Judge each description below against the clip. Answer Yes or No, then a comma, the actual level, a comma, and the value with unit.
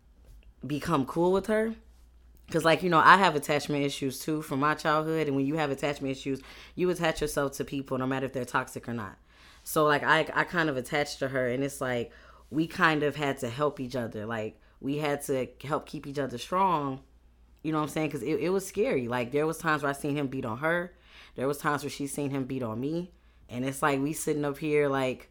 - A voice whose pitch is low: No, medium, 145 Hz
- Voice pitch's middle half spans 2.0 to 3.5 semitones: Yes, average, 2.9 semitones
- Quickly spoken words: Yes, fast, 240 wpm